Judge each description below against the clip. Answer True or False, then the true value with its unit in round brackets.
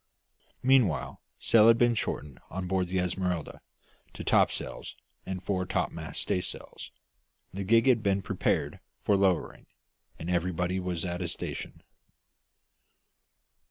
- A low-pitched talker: True (95 Hz)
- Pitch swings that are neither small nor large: False (2.2 semitones)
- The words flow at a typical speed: False (125 wpm)